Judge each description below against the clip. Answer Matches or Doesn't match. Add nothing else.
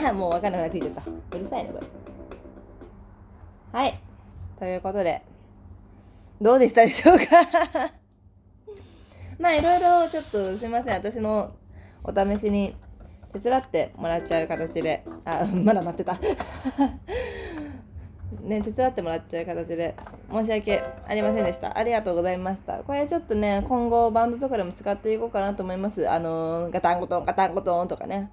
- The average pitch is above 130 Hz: Matches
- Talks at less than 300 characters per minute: Doesn't match